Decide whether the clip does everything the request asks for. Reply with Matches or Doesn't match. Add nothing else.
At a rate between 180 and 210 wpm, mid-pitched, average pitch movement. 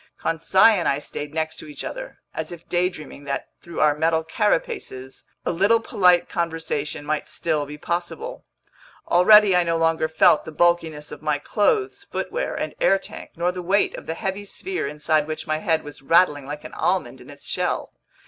Matches